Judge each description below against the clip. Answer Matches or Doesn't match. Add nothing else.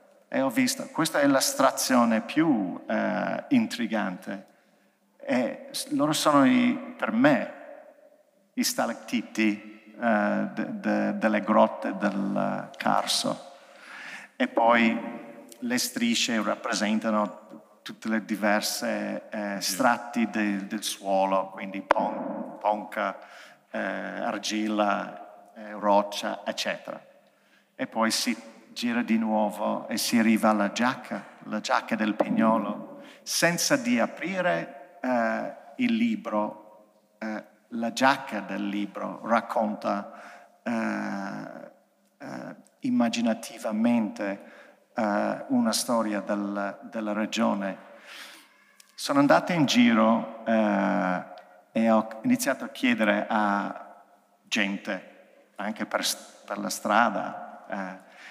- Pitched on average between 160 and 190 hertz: Doesn't match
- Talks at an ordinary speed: Doesn't match